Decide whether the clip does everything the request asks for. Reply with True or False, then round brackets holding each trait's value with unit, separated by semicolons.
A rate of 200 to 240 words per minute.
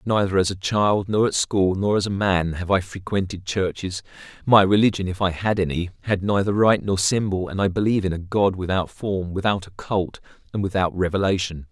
True (205 wpm)